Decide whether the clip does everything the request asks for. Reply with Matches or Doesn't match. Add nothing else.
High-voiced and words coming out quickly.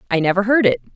Matches